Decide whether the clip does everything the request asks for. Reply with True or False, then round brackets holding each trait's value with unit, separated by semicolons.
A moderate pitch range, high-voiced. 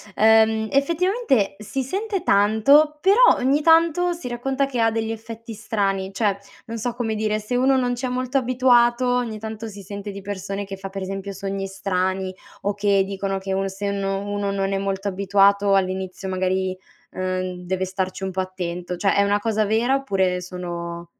True (3.9 semitones; 205 Hz)